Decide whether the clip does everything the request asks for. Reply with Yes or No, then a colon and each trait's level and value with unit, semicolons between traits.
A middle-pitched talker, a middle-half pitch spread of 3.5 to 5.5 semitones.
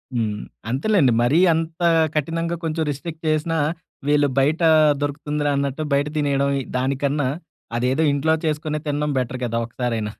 No: medium, 145 Hz; average, 3.0 semitones